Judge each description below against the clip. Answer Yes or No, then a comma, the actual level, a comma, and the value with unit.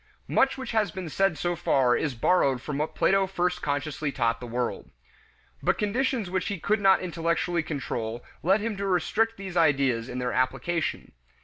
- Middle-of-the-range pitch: Yes, medium, 170 Hz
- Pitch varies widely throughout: Yes, wide, 6.3 semitones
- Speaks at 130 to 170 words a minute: No, average, 180 wpm